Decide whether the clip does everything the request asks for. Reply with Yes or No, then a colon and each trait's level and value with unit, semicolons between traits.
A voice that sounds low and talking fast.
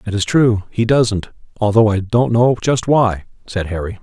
No: low, 110 Hz; average, 195 wpm